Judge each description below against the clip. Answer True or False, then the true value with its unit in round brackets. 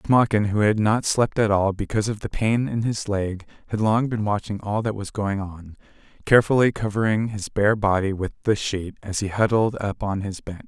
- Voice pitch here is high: False (105 Hz)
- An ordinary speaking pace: False (215 wpm)